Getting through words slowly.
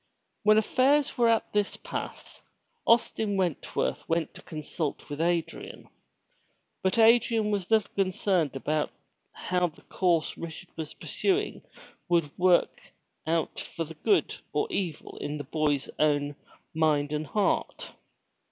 Yes: slow, 125 wpm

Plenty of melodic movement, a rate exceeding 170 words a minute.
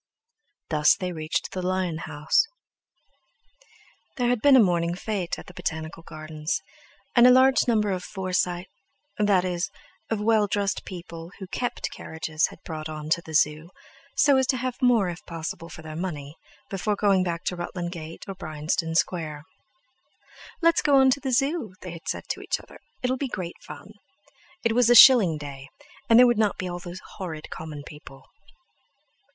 Yes: wide, 5.8 semitones; average, 180 wpm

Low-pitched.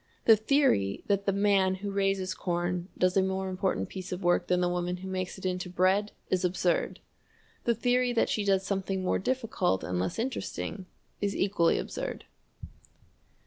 No: high, 190 Hz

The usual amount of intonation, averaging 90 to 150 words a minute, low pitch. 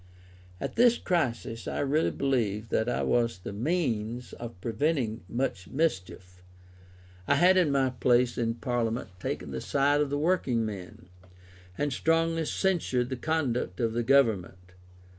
Yes: average, 4.7 semitones; average, 145 wpm; low, 125 Hz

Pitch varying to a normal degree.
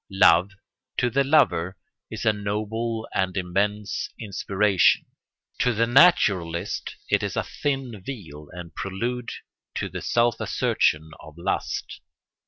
Yes: average, 4.7 semitones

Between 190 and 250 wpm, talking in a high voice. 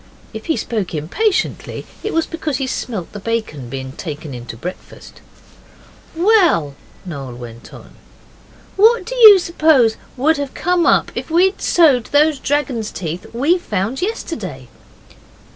No: average, 145 wpm; very high, 250 Hz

